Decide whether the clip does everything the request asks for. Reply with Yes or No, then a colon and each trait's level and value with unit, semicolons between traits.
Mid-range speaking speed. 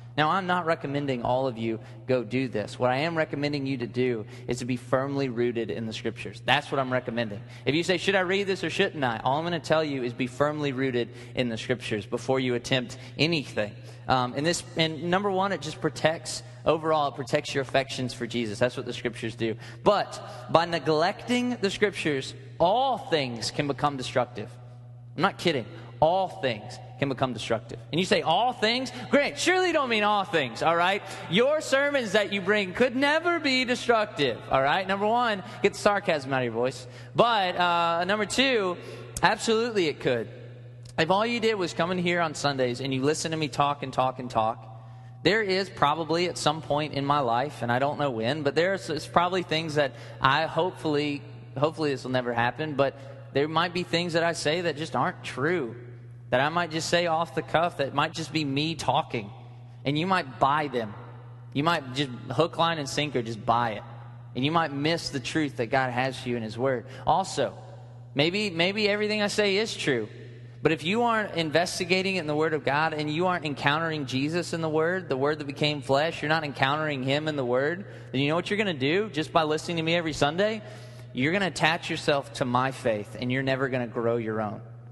No: fast, 215 wpm